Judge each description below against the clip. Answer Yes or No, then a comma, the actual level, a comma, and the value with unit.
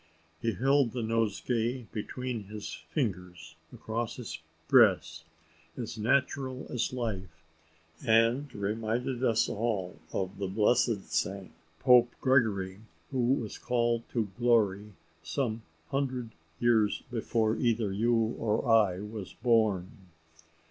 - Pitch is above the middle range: No, low, 115 Hz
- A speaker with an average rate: No, slow, 115 wpm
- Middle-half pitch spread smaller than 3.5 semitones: Yes, average, 3.1 semitones